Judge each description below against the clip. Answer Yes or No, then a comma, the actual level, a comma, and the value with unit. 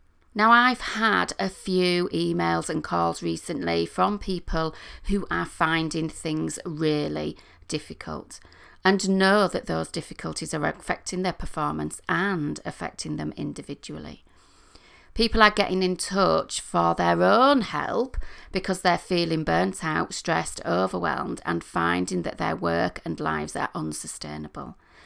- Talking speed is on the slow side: Yes, slow, 130 wpm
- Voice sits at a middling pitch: Yes, medium, 165 Hz